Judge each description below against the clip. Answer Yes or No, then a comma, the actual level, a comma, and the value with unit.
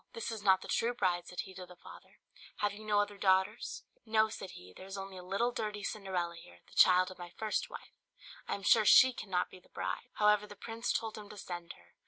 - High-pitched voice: Yes, high, 200 Hz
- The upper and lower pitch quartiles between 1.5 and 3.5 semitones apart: Yes, average, 2.8 semitones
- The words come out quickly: Yes, fast, 245 wpm